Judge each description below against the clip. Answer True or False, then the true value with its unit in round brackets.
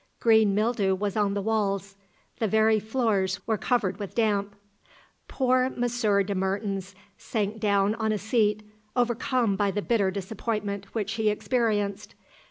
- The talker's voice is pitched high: True (210 Hz)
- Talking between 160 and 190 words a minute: False (145 wpm)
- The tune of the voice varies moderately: False (1.9 semitones)